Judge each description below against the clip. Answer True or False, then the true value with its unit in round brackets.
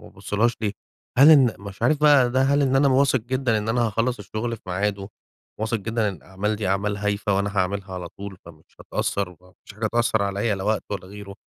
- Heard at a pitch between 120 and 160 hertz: False (105 Hz)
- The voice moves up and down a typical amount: True (3.3 semitones)